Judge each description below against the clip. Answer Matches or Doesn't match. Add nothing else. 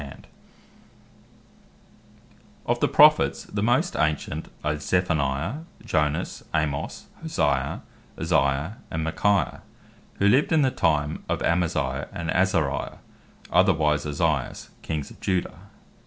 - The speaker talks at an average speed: Doesn't match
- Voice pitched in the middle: Doesn't match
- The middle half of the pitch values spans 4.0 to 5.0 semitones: Matches